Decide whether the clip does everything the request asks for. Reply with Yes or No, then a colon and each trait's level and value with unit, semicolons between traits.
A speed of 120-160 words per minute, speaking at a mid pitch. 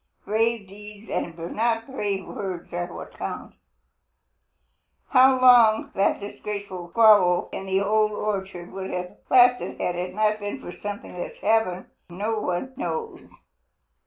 No: slow, 135 wpm; high, 205 Hz